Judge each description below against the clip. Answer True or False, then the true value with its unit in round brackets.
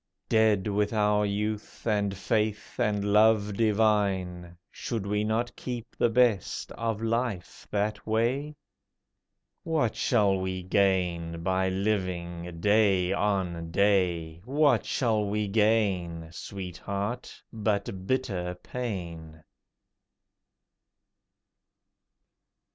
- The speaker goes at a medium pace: False (95 wpm)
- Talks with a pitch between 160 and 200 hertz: False (100 Hz)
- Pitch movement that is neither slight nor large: True (3.0 semitones)